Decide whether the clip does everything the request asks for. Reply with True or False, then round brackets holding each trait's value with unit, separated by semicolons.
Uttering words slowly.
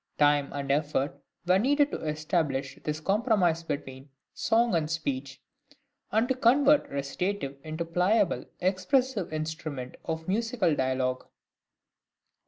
True (120 wpm)